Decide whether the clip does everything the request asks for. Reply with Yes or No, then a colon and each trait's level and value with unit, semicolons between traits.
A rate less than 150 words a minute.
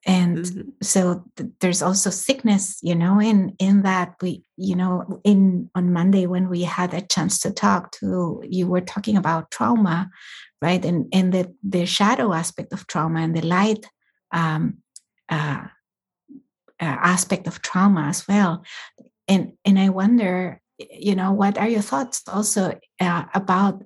No: average, 160 wpm